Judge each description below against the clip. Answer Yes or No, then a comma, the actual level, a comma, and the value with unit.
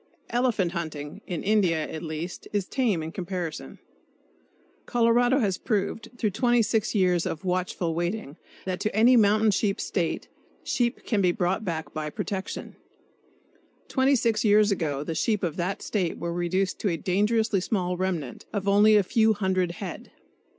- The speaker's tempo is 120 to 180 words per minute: Yes, average, 155 wpm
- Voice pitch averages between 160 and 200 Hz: Yes, high, 190 Hz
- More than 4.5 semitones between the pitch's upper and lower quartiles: No, average, 3.9 semitones